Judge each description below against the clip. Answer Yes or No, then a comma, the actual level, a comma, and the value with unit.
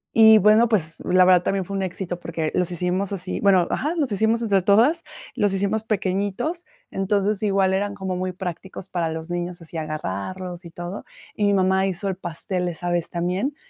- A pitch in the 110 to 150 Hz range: No, high, 190 Hz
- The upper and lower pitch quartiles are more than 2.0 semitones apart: Yes, narrow, 2.4 semitones